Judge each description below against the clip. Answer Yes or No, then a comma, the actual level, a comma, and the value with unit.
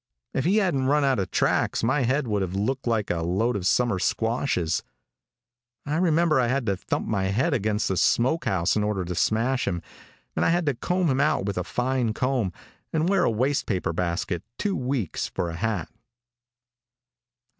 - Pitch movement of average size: No, wide, 6.2 semitones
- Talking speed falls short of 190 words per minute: No, average, 195 wpm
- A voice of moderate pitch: No, low, 115 Hz